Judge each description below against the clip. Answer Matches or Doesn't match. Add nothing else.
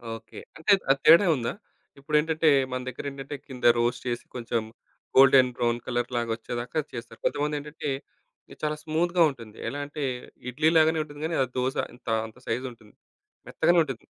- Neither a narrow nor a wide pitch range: Matches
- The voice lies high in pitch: Doesn't match